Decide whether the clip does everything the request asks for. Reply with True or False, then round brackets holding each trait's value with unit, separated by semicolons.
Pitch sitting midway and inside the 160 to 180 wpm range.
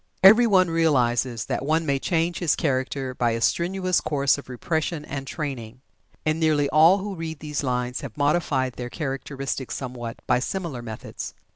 True (145 Hz; 165 wpm)